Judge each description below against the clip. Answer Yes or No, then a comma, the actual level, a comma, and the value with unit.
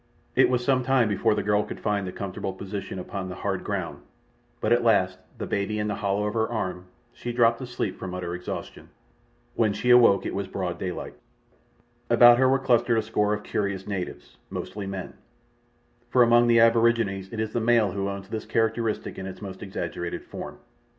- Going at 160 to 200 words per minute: Yes, average, 190 wpm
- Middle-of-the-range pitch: No, low, 105 Hz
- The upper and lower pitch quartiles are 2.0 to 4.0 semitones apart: Yes, average, 3.3 semitones